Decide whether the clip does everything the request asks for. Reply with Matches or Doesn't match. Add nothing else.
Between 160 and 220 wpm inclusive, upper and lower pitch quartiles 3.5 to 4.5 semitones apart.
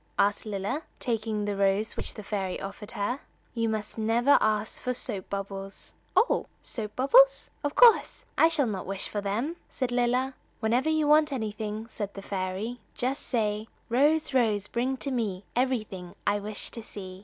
Matches